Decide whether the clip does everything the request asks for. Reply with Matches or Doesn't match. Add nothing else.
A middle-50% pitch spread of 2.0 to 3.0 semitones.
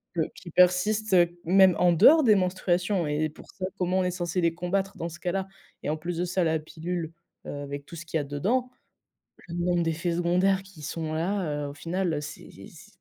Matches